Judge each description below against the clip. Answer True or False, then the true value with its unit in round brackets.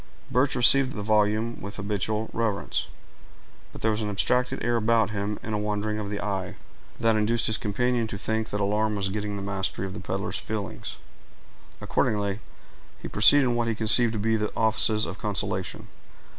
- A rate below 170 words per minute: False (185 wpm)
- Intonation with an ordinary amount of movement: False (1.7 semitones)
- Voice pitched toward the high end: False (105 Hz)